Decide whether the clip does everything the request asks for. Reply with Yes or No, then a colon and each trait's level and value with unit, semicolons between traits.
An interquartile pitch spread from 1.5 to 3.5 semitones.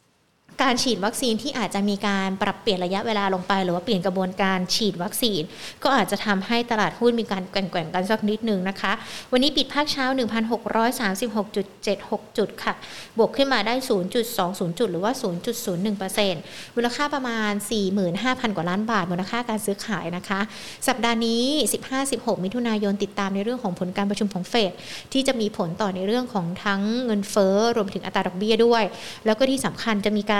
Yes: average, 3.2 semitones